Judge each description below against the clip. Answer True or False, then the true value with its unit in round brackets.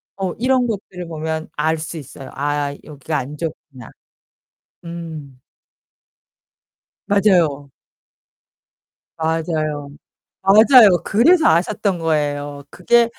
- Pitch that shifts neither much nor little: True (4.9 semitones)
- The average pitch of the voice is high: False (160 Hz)